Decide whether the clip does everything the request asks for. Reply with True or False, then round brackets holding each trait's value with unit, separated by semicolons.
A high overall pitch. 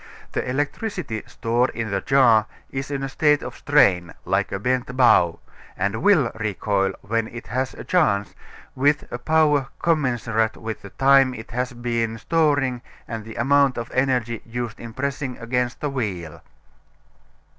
False (120 Hz)